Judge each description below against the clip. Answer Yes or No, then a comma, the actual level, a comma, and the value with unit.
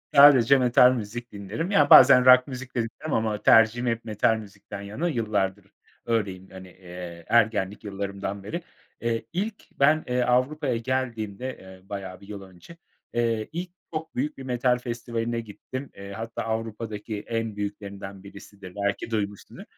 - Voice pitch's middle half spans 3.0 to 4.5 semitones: Yes, average, 4.0 semitones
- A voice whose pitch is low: Yes, low, 115 Hz